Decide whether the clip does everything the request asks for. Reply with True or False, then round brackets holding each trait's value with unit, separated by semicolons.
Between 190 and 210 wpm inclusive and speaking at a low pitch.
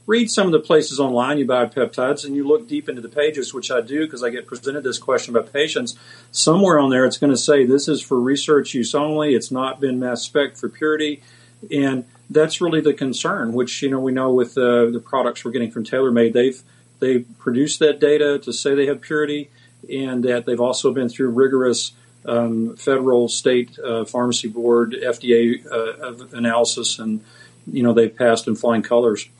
True (200 wpm; 125 Hz)